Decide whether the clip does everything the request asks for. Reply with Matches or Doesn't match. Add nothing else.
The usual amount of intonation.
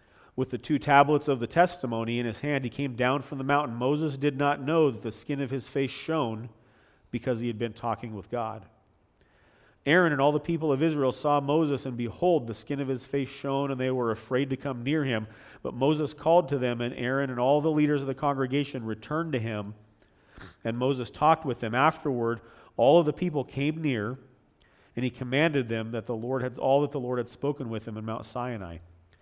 Matches